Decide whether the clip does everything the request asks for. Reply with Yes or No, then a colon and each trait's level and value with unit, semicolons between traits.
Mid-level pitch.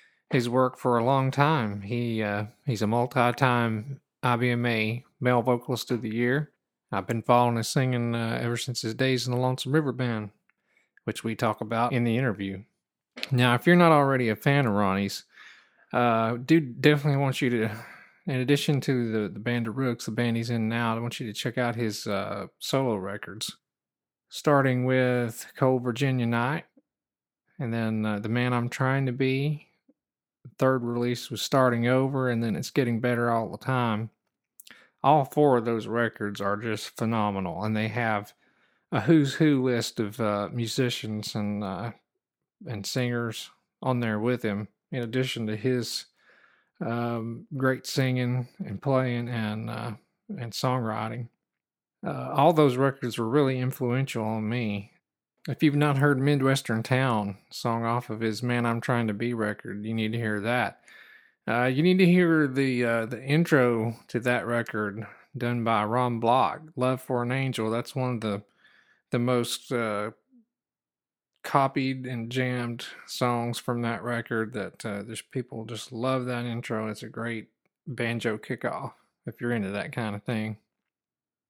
No: low, 120 Hz